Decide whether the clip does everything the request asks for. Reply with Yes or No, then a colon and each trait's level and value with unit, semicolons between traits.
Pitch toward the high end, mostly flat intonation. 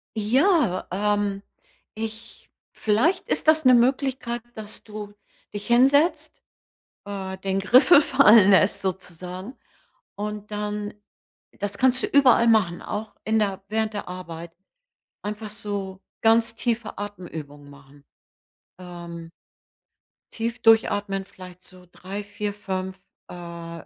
No: high, 205 Hz; average, 3.3 semitones